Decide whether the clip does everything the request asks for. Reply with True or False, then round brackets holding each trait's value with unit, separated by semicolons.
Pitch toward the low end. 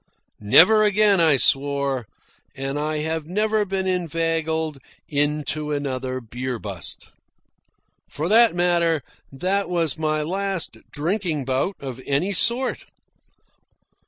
False (160 Hz)